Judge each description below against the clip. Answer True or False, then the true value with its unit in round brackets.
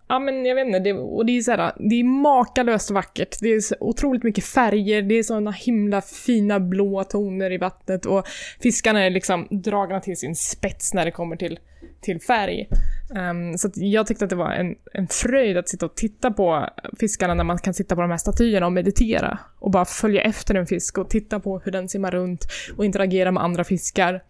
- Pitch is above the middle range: True (195 Hz)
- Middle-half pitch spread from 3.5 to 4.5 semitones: False (3.1 semitones)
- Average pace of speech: False (215 wpm)